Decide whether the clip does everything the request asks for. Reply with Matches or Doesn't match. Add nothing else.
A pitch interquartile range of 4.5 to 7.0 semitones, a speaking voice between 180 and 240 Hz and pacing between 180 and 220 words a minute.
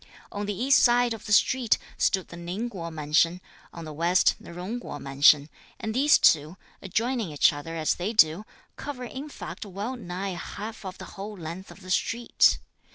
Matches